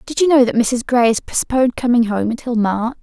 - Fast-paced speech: Yes, fast, 240 wpm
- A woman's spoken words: Yes, female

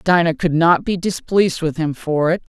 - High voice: No, medium, 170 Hz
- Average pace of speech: No, fast, 210 wpm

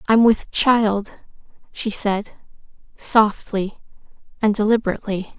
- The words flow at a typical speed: No, slow, 90 wpm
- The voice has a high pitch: Yes, high, 210 Hz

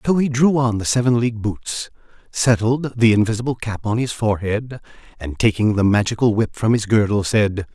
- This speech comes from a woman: No, male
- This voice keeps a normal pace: Yes, average, 185 wpm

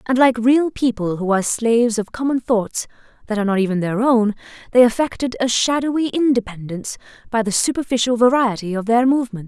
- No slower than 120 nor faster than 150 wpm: No, average, 175 wpm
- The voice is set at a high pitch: Yes, high, 235 Hz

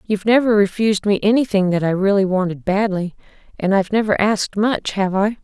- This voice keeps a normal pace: Yes, average, 190 wpm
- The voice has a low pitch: No, high, 200 Hz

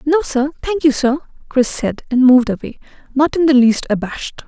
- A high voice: Yes, very high, 270 Hz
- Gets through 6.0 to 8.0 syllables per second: No, 5.4 syllables/s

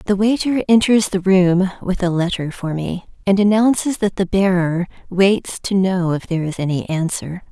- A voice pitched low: No, high, 190 Hz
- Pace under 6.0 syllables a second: Yes, 4.8 syllables/s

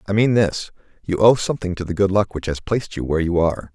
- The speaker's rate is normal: No, fast, 275 wpm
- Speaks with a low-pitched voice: Yes, very low, 95 Hz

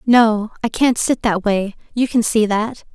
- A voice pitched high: Yes, high, 225 Hz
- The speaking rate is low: No, fast, 205 wpm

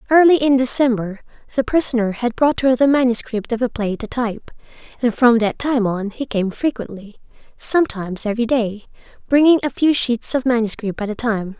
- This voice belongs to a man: No, female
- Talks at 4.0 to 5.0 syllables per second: No, 5.5 syllables/s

